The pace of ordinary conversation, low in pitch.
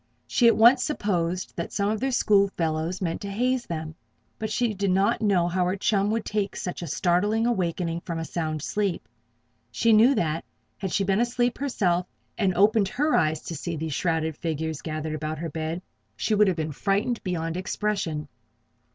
No: average, 185 wpm; medium, 185 Hz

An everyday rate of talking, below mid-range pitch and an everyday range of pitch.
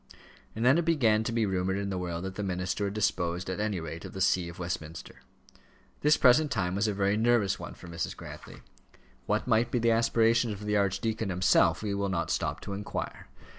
No: fast, 215 wpm; low, 100 Hz; average, 3.5 semitones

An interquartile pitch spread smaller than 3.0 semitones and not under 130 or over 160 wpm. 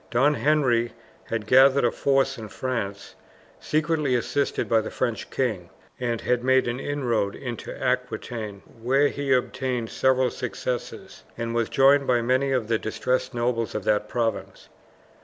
Yes: narrow, 2.5 semitones; average, 150 wpm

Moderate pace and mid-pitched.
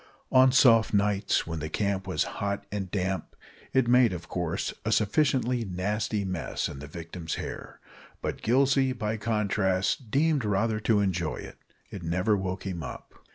No: average, 160 wpm; low, 100 Hz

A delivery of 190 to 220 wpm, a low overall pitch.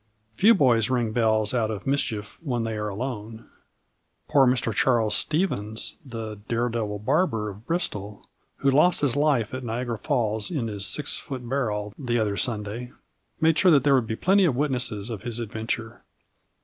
No: average, 170 wpm; low, 120 Hz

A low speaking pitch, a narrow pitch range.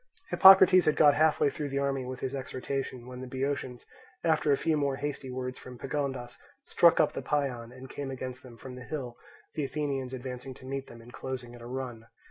Yes: low, 130 Hz; narrow, 2.0 semitones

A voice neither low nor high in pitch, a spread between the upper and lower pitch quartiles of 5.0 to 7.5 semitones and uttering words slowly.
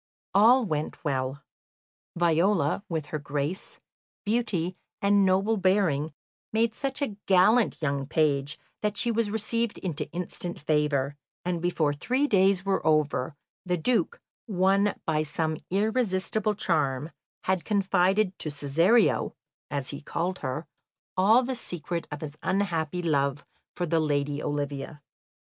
Yes: medium, 175 Hz; average, 5.3 semitones; slow, 130 wpm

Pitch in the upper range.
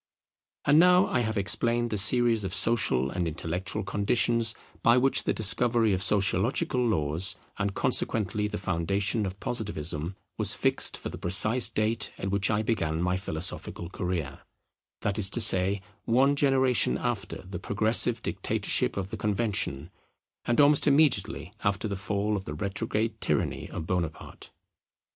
No: low, 100 Hz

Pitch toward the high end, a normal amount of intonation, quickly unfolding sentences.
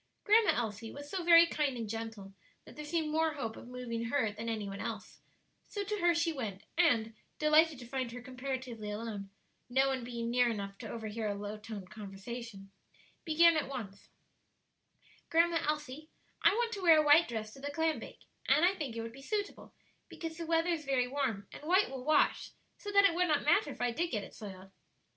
No: very high, 260 Hz; wide, 6.3 semitones; fast, 210 wpm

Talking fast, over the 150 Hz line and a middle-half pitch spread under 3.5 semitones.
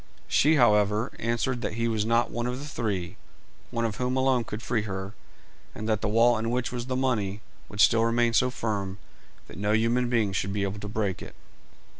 No: fast, 210 wpm; low, 115 Hz; average, 2.7 semitones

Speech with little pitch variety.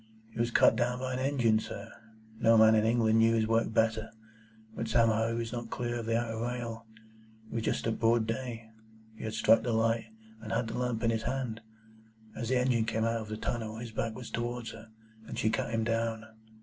Yes: narrow, 1.0 semitones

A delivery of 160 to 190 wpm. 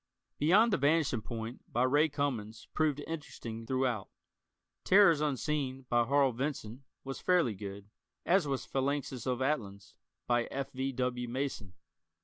No: average, 140 wpm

